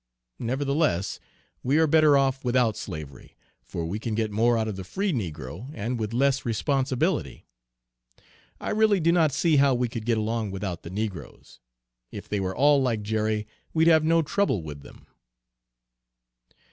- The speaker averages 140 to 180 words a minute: Yes, average, 165 wpm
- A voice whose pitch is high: No, low, 120 Hz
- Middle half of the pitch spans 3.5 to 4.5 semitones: No, wide, 5.6 semitones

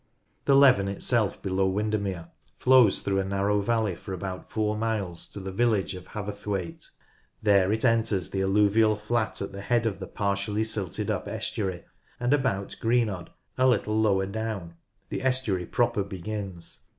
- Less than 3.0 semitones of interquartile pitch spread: Yes, narrow, 2.5 semitones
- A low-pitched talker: Yes, low, 100 Hz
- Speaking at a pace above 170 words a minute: No, average, 160 wpm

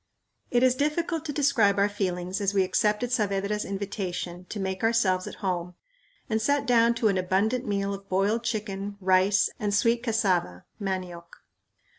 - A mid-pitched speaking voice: No, high, 200 Hz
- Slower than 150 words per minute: No, average, 160 wpm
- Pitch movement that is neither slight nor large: Yes, average, 3.4 semitones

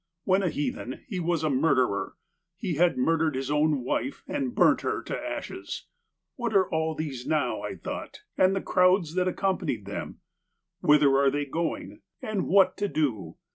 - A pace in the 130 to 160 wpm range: No, average, 175 wpm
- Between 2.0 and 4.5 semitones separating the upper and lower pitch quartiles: No, average, 4.9 semitones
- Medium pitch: Yes, medium, 160 Hz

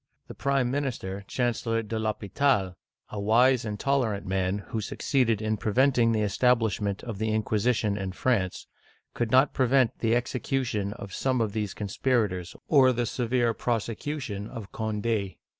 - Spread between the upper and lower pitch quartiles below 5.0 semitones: Yes, average, 3.5 semitones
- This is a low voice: Yes, low, 115 Hz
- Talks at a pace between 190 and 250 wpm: No, average, 155 wpm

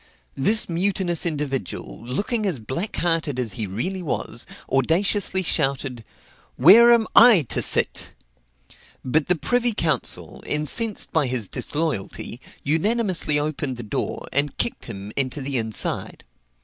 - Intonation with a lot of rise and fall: Yes, wide, 6.6 semitones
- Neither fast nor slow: No, slow, 125 wpm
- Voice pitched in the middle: Yes, medium, 155 Hz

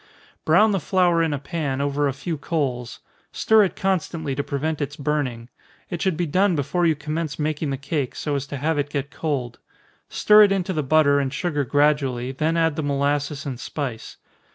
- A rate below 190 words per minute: No, average, 200 wpm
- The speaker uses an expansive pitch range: No, average, 2.9 semitones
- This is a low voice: No, medium, 145 Hz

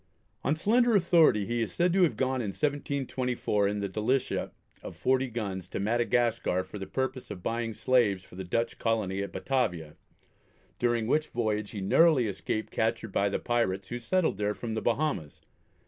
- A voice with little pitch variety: No, average, 4.5 semitones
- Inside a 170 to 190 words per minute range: Yes, average, 180 wpm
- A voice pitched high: No, low, 115 Hz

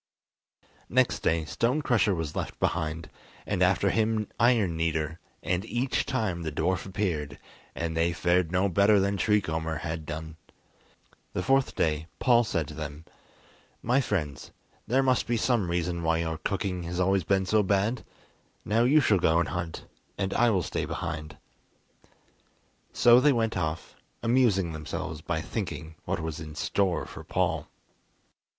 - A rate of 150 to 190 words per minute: Yes, average, 155 wpm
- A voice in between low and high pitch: No, very low, 90 Hz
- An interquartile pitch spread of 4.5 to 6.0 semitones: Yes, average, 5.1 semitones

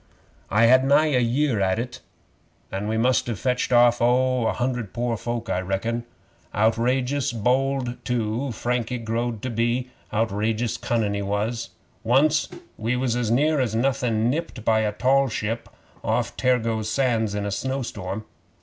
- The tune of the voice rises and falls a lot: No, narrow, 2.5 semitones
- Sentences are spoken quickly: No, average, 160 wpm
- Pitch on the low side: Yes, low, 120 Hz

